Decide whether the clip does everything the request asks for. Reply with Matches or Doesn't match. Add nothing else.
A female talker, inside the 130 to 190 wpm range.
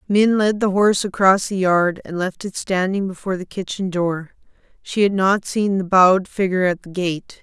Doesn't match